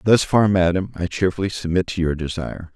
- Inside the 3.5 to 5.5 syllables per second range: No, 5.8 syllables/s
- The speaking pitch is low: Yes, very low, 90 Hz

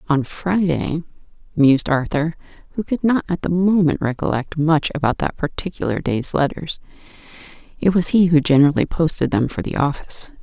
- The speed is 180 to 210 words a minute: No, average, 155 wpm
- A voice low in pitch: No, medium, 160 Hz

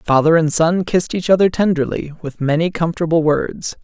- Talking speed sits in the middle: Yes, average, 170 wpm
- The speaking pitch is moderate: Yes, medium, 165 Hz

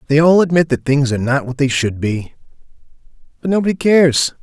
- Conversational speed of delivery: Yes, average, 175 wpm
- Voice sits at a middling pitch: Yes, medium, 145 Hz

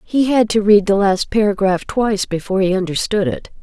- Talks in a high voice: Yes, high, 200 Hz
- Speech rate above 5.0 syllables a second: Yes, 5.5 syllables/s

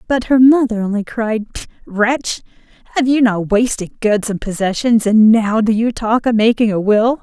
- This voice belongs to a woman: Yes, female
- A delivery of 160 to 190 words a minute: Yes, average, 185 wpm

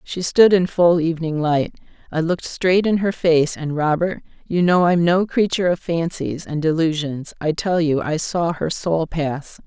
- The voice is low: No, medium, 165 Hz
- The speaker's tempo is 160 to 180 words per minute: No, average, 190 wpm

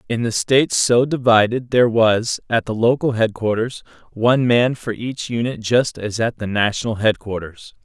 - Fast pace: No, average, 170 wpm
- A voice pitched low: Yes, low, 115 Hz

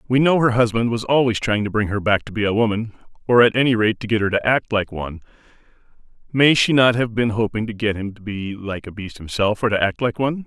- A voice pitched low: Yes, low, 110 Hz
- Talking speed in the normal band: No, fast, 265 wpm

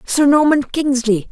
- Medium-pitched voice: No, very high, 270 Hz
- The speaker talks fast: No, slow, 135 wpm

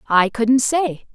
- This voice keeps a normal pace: Yes, average, 155 wpm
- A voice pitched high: Yes, high, 240 Hz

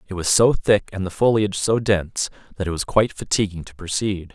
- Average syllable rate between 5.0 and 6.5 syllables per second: Yes, 5.9 syllables/s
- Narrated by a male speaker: Yes, male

